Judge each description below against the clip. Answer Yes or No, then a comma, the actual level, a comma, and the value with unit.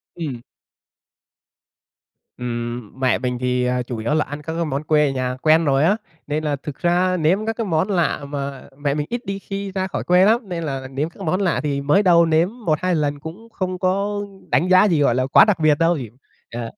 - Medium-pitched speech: Yes, medium, 155 Hz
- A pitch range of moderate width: Yes, average, 4.9 semitones